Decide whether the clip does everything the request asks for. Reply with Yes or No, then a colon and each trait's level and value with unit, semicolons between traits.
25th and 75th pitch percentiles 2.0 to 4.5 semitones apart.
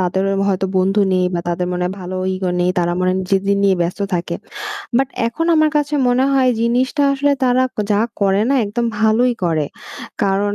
No: average, 5.3 semitones